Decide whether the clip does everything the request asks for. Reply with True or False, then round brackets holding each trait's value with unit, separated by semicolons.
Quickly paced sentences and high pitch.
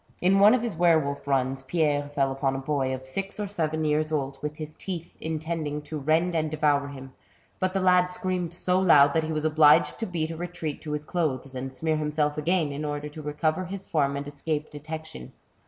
False (220 wpm; 155 Hz)